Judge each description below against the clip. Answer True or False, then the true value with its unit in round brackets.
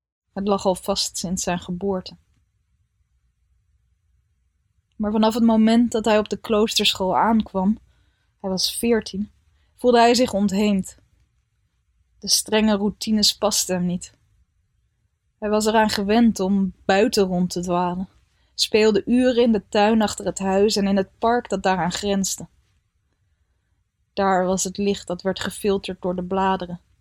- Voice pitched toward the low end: False (190 Hz)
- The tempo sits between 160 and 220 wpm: False (140 wpm)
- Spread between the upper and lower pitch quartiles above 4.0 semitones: True (4.4 semitones)